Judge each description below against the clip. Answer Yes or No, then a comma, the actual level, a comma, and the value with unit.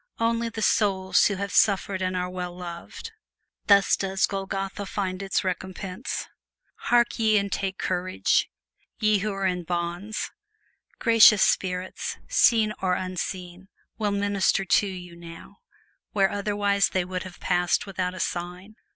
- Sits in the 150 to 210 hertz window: Yes, high, 190 Hz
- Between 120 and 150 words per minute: Yes, average, 140 wpm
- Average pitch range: No, narrow, 2.0 semitones